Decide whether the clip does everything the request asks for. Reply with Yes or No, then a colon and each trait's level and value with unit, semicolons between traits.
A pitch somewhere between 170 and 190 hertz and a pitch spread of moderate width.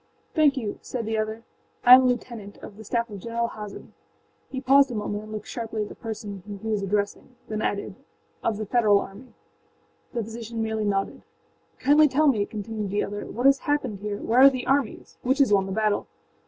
No: high, 220 Hz; average, 3.4 semitones